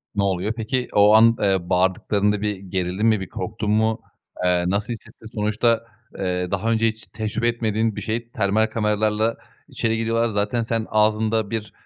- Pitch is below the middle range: Yes, low, 110 Hz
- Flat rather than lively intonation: Yes, narrow, 2.1 semitones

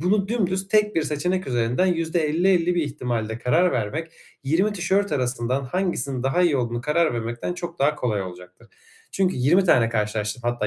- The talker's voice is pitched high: No, medium, 150 Hz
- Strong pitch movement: Yes, wide, 6.9 semitones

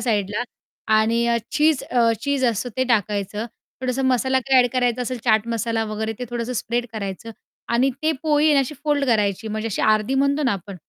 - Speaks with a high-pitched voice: Yes, high, 240 Hz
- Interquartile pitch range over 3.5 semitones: No, average, 3.2 semitones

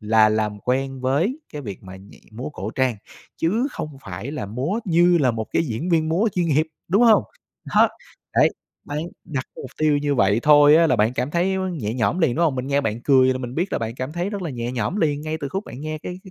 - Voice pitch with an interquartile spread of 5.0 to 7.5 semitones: Yes, wide, 5.6 semitones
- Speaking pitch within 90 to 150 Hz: Yes, medium, 140 Hz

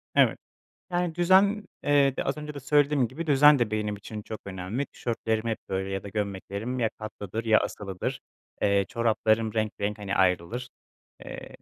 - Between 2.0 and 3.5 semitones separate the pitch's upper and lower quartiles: No, wide, 5.5 semitones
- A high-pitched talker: No, low, 110 Hz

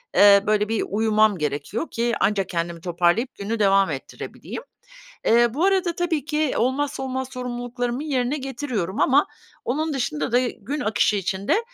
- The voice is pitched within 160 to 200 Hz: No, high, 235 Hz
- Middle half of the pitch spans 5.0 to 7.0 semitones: Yes, average, 5.3 semitones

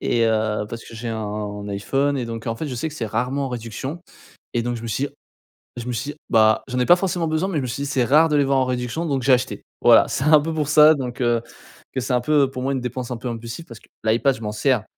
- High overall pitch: No, low, 125 Hz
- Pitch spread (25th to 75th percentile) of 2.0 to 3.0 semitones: No, average, 3.6 semitones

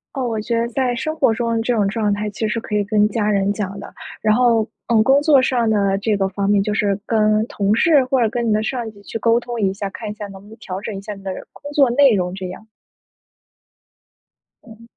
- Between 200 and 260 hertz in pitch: Yes, high, 215 Hz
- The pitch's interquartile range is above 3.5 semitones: No, average, 2.7 semitones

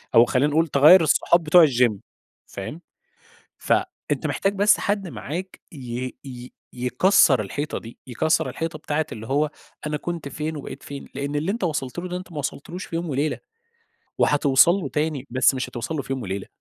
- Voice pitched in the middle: Yes, medium, 150 Hz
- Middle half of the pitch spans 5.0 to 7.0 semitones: No, average, 4.3 semitones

